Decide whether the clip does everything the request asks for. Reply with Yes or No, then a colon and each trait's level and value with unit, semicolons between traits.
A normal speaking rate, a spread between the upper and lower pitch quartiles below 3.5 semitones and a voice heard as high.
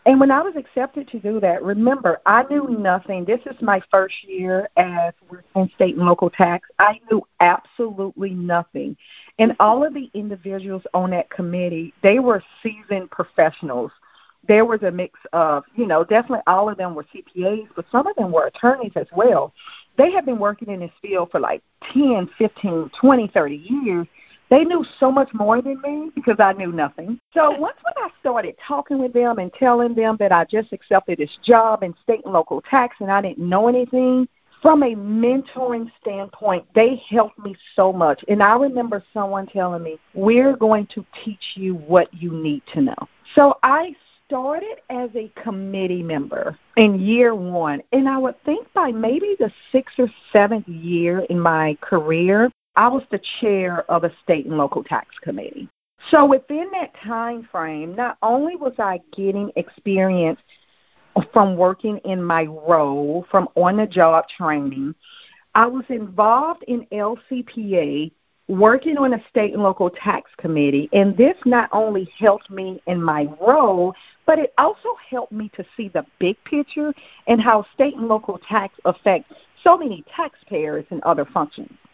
No: average, 175 wpm; wide, 5.6 semitones; high, 210 Hz